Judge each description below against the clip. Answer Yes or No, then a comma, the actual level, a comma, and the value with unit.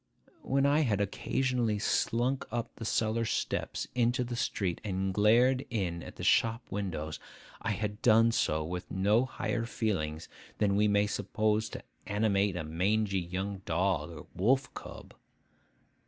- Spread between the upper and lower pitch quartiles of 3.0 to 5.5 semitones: Yes, average, 3.5 semitones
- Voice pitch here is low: Yes, low, 105 Hz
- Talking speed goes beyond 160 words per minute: No, average, 145 wpm